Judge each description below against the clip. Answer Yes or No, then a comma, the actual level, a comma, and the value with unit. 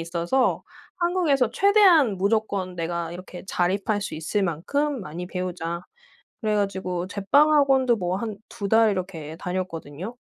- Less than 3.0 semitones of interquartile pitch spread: No, average, 5.3 semitones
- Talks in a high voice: Yes, high, 195 Hz